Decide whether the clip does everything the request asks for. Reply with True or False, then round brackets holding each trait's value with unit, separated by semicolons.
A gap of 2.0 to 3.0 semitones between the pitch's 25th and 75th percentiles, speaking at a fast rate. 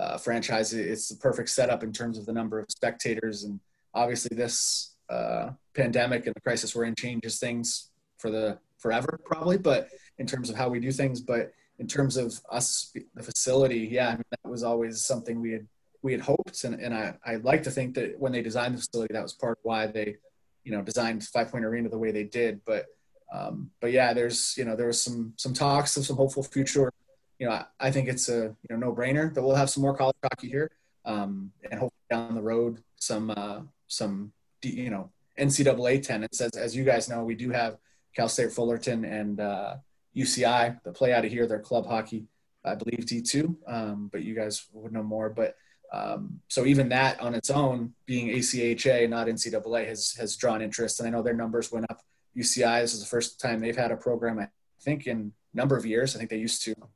True (2.6 semitones; 220 wpm)